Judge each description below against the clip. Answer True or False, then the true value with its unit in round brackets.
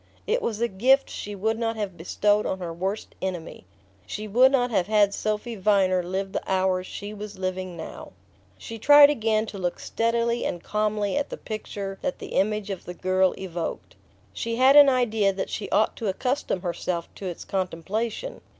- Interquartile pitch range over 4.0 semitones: False (3.4 semitones)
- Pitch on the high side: True (205 Hz)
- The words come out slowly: False (185 wpm)